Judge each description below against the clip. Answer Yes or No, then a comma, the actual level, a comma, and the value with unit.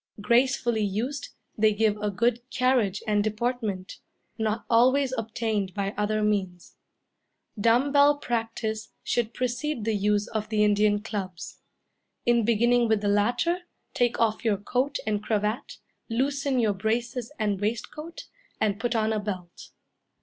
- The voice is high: Yes, high, 220 Hz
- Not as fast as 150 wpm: Yes, average, 140 wpm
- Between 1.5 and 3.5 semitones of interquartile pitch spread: Yes, narrow, 2.6 semitones